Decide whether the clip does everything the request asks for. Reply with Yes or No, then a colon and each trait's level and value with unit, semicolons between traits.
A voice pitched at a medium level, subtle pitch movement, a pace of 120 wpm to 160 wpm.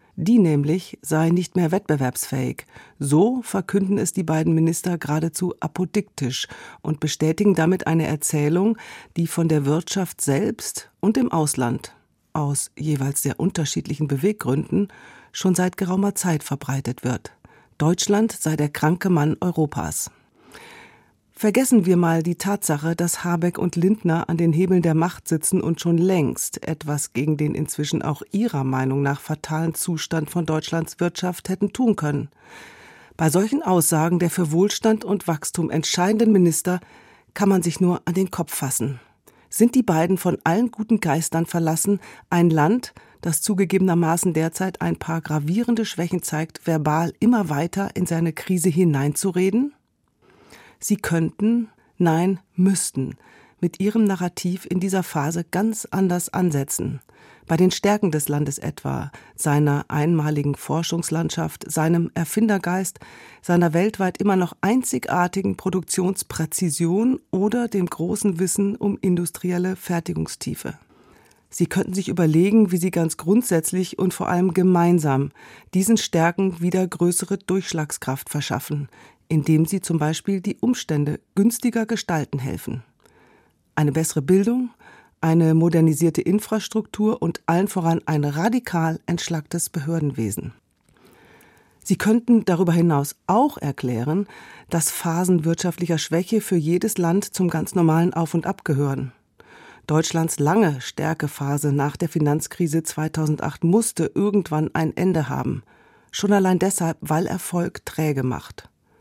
No: medium, 170 Hz; average, 3.5 semitones; average, 130 wpm